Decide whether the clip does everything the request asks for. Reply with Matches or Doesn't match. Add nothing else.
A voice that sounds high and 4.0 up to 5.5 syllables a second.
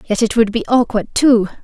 Matches